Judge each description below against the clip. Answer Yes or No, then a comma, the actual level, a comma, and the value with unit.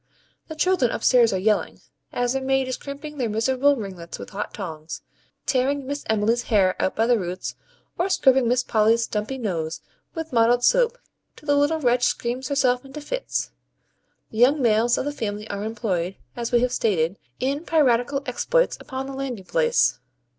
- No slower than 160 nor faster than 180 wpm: Yes, average, 175 wpm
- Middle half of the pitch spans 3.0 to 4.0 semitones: No, average, 4.4 semitones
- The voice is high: Yes, high, 245 Hz